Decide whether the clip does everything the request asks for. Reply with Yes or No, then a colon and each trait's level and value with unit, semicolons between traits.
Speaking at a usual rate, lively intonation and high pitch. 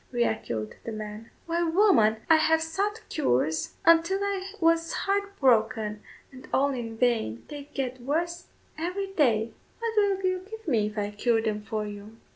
Yes: average, 170 wpm; wide, 8.3 semitones; very high, 270 Hz